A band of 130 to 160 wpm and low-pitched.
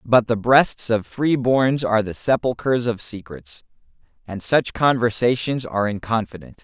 Yes: average, 155 wpm; low, 115 Hz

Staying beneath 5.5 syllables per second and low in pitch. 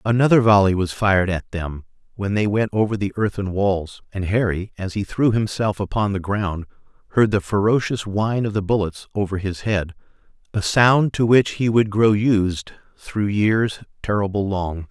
Yes: 4.7 syllables/s; low, 100 Hz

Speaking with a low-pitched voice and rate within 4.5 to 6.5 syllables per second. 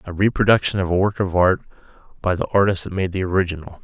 No: very low, 95 Hz; 6.8 syllables/s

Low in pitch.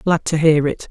No: medium, 160 Hz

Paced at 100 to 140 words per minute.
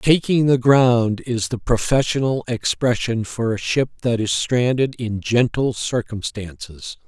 Yes: slow, 135 wpm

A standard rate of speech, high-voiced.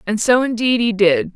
No: fast, 220 wpm; high, 220 Hz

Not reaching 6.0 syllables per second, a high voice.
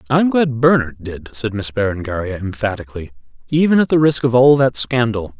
No: 5.7 syllables/s; low, 120 Hz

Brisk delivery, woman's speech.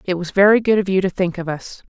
Yes: fast, 315 wpm; female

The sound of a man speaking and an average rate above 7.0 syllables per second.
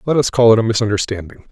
Yes: male; 7.3 syllables/s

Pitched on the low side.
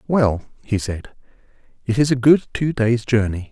Yes: low, 120 Hz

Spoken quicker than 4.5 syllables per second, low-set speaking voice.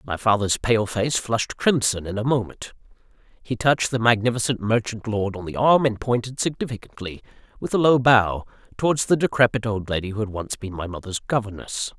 Yes: 5.5 syllables/s; low, 115 Hz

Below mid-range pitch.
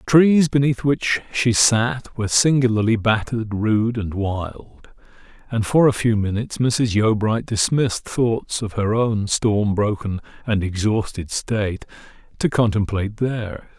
Yes: low, 110 Hz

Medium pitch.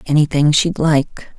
Yes: medium, 150 Hz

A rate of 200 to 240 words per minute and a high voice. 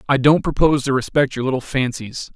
No: fast, 205 wpm; low, 135 Hz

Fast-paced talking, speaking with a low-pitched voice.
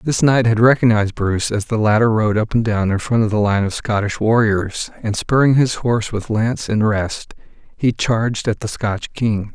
Yes: fast, 215 wpm; low, 110 Hz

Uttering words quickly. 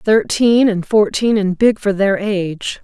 No: average, 170 wpm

